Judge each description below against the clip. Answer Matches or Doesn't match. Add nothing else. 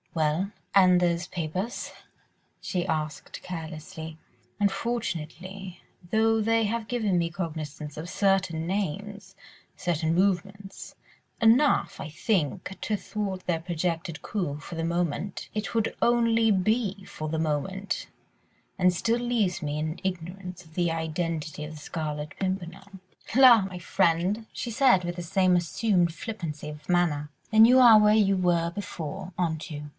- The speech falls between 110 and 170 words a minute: Matches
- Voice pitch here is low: Doesn't match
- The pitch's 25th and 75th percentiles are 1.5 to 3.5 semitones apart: Doesn't match